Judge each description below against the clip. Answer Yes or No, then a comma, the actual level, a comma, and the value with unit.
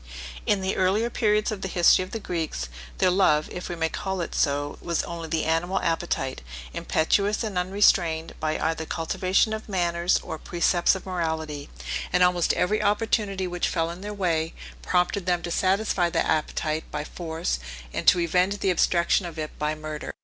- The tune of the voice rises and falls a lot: No, average, 2.9 semitones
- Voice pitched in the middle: Yes, medium, 175 Hz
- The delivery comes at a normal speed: Yes, average, 180 wpm